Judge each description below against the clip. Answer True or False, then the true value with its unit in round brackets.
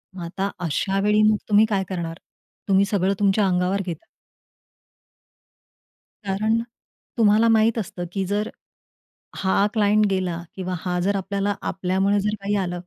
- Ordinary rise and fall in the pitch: False (2.1 semitones)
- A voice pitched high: True (195 Hz)